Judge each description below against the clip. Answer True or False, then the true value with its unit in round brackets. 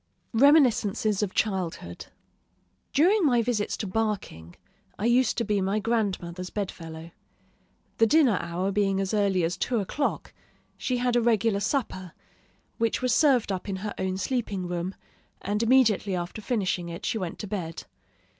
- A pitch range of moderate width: True (4.1 semitones)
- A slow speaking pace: False (155 wpm)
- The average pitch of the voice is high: True (205 Hz)